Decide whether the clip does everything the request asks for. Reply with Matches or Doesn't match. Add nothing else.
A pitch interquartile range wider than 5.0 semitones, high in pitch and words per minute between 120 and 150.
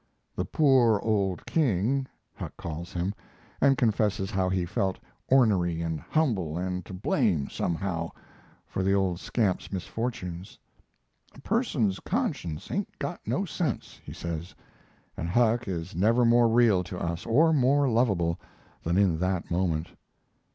Doesn't match